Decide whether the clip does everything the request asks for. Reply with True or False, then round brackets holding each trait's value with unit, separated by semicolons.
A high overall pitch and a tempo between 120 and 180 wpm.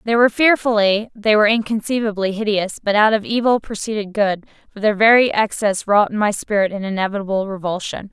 True (210 Hz; 170 wpm)